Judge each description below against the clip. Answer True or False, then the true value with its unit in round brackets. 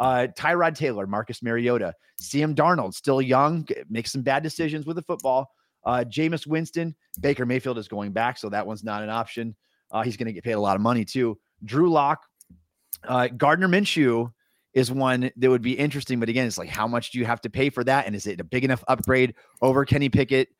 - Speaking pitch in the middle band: False (130 Hz)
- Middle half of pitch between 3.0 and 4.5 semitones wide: True (3.4 semitones)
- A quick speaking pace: True (220 wpm)